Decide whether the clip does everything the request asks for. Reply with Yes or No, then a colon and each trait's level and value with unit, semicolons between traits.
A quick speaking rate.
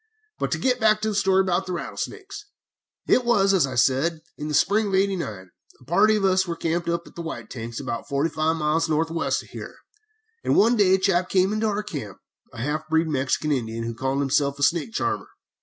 Yes: fast, 220 wpm